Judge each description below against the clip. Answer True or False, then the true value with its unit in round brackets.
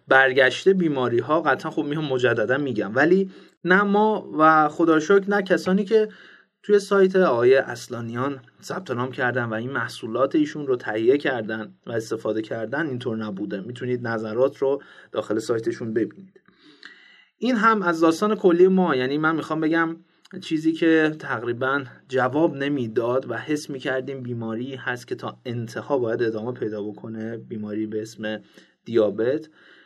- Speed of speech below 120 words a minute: False (145 wpm)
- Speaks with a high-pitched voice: False (140 Hz)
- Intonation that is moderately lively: False (6.8 semitones)